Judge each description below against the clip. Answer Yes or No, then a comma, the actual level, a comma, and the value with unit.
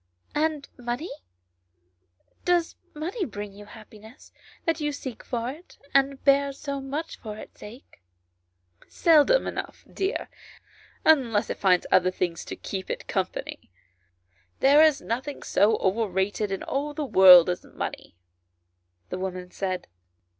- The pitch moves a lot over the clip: Yes, wide, 7.5 semitones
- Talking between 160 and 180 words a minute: No, average, 145 wpm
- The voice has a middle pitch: No, high, 240 Hz